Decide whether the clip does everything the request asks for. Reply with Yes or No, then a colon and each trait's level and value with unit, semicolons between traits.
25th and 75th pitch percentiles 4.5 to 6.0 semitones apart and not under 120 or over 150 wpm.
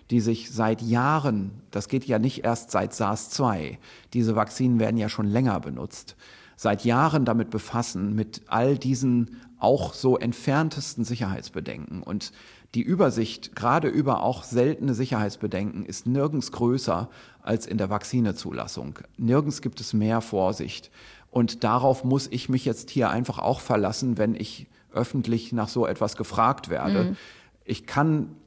No: average, 2.9 semitones; average, 145 wpm